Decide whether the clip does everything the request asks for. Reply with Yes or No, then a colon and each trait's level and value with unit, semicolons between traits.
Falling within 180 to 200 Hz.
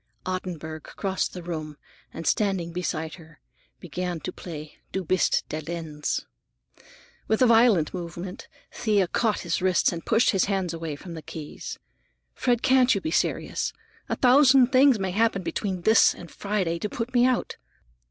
Yes: medium, 185 Hz